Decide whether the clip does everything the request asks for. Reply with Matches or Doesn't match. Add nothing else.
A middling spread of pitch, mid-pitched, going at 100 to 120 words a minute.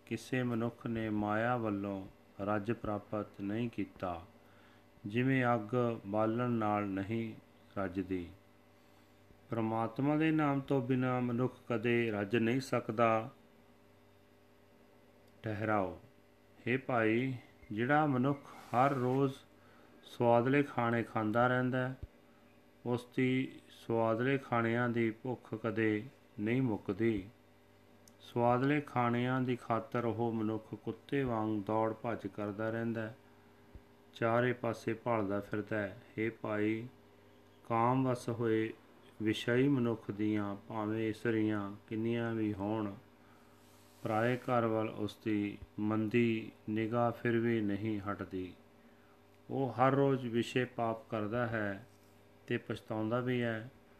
Doesn't match